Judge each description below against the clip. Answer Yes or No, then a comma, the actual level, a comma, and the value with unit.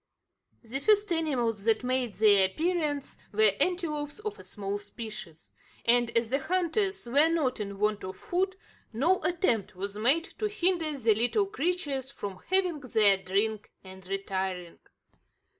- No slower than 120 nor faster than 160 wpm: Yes, average, 145 wpm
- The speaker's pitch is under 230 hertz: No, very high, 250 Hz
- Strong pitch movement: Yes, wide, 8.6 semitones